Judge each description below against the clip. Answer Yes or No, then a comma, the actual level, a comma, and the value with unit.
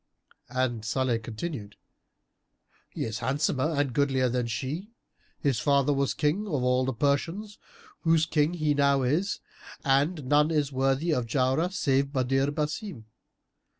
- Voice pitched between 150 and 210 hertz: No, medium, 140 Hz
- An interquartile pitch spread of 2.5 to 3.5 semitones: Yes, average, 3.1 semitones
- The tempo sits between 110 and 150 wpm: Yes, average, 140 wpm